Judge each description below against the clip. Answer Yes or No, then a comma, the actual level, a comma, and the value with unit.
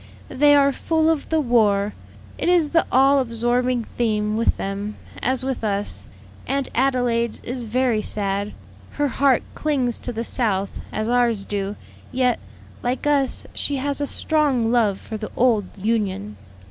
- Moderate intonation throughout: Yes, average, 4.2 semitones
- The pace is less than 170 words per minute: Yes, average, 155 wpm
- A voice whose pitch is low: No, high, 240 Hz